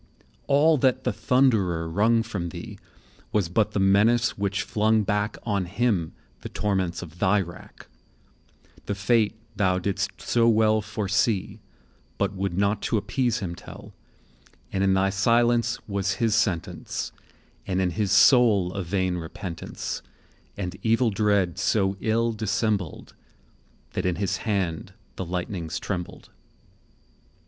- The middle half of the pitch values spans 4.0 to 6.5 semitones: No, average, 3.1 semitones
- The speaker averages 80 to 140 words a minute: Yes, slow, 135 wpm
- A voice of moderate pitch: No, low, 100 Hz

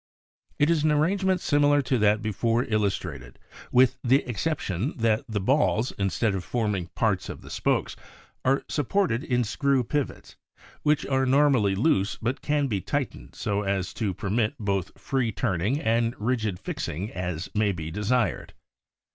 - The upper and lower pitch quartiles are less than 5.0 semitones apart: No, wide, 5.4 semitones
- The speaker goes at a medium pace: Yes, average, 160 wpm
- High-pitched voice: No, low, 115 Hz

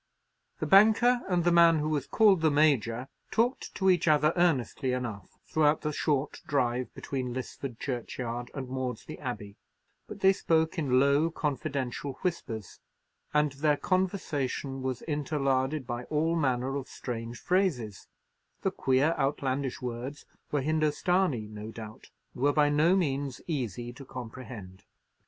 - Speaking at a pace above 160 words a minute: No, average, 140 wpm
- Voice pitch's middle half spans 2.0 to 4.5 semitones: Yes, average, 4.1 semitones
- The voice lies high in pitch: No, medium, 140 Hz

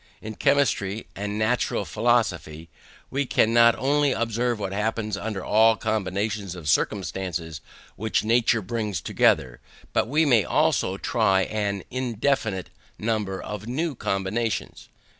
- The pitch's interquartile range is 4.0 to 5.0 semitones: No, average, 3.3 semitones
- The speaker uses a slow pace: Yes, slow, 130 wpm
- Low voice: Yes, low, 110 Hz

